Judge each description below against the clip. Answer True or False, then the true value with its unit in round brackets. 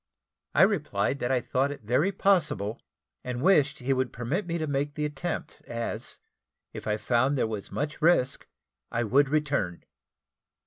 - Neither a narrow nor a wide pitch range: True (4.0 semitones)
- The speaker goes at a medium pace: True (165 wpm)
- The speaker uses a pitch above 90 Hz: True (140 Hz)